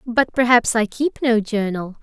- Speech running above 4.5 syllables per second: No, 4.4 syllables/s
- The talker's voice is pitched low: No, high, 230 Hz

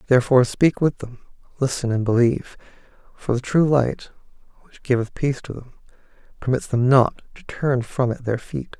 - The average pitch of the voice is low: Yes, low, 130 Hz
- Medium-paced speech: Yes, average, 170 wpm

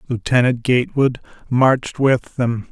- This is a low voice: Yes, low, 125 Hz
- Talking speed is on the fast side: No, slow, 110 wpm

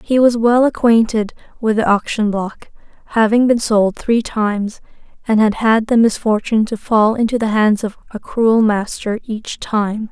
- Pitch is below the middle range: No, high, 220 Hz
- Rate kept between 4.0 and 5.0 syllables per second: Yes, 4.5 syllables/s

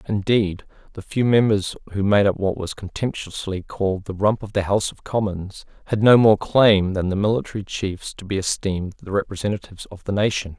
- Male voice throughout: Yes, male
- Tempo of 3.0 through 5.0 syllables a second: No, 5.5 syllables/s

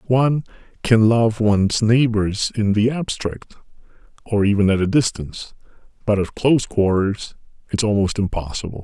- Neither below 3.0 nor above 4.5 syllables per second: No, 5.0 syllables/s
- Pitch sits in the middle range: No, low, 110 Hz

